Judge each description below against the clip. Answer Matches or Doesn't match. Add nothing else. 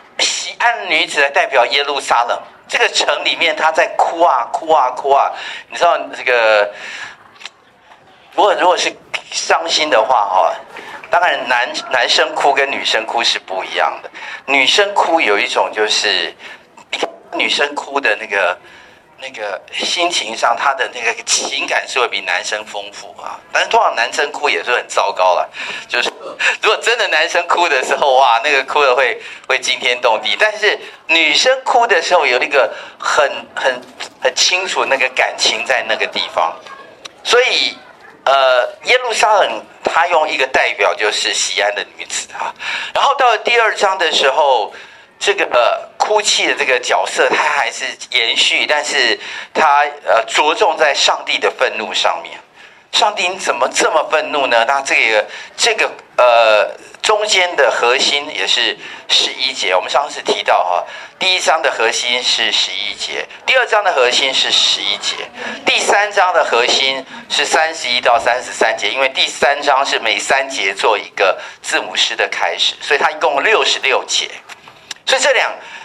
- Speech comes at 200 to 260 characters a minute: Matches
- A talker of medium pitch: Matches